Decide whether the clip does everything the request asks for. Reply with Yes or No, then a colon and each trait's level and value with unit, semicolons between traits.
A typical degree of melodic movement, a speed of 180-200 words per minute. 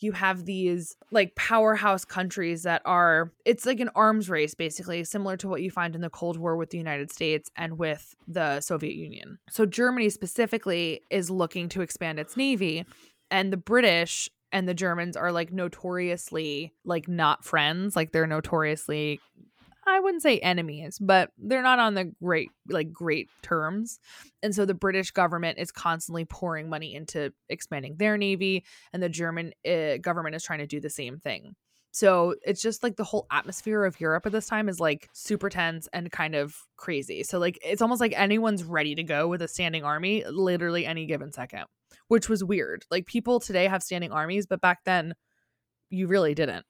Yes: average, 3.8 semitones; average, 190 wpm